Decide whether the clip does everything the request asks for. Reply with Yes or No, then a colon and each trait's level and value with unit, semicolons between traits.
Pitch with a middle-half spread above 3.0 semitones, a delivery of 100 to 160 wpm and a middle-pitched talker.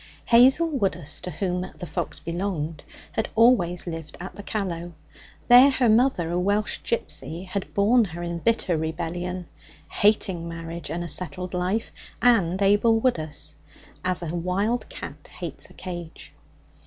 Yes: average, 4.1 semitones; average, 145 wpm; medium, 180 Hz